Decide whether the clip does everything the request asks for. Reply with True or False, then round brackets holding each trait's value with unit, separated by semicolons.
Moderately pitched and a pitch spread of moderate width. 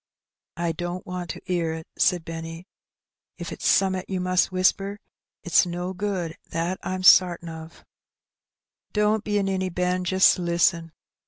False (180 Hz; 1.8 semitones)